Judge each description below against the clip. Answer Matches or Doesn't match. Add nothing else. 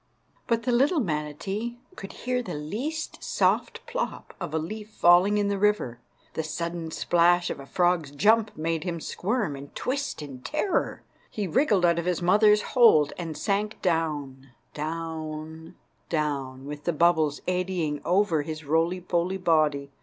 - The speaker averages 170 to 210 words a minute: Doesn't match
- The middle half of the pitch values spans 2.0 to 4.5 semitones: Doesn't match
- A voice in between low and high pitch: Matches